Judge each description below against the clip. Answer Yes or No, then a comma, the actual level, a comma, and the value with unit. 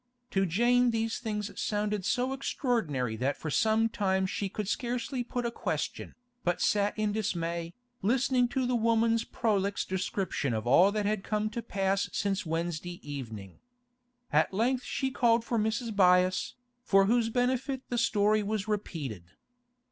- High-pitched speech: Yes, high, 210 Hz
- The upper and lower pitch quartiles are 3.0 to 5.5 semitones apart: Yes, average, 4.2 semitones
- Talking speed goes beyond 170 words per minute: No, average, 155 wpm